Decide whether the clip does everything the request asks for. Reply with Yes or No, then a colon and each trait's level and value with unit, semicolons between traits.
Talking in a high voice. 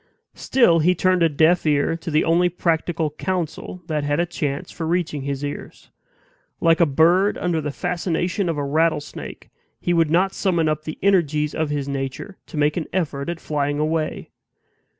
No: medium, 160 Hz